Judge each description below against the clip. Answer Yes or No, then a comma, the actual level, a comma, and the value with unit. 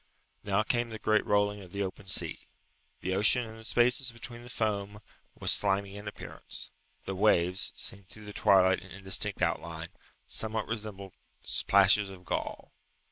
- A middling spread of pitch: No, narrow, 2.1 semitones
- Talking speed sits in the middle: Yes, average, 160 wpm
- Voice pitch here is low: Yes, low, 105 Hz